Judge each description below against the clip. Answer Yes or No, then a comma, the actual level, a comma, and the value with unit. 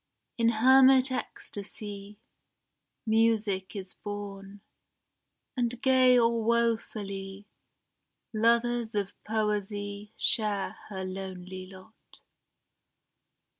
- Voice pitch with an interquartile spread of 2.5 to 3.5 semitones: Yes, average, 2.9 semitones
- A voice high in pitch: Yes, high, 210 Hz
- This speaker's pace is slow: Yes, slow, 75 wpm